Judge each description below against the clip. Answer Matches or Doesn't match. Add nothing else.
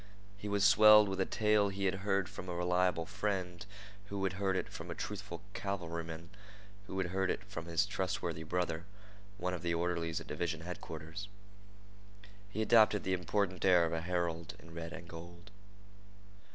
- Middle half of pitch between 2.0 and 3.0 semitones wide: Matches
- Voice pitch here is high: Doesn't match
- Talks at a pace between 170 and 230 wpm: Matches